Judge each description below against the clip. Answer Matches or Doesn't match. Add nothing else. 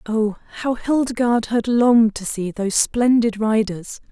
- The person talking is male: Doesn't match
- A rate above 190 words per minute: Doesn't match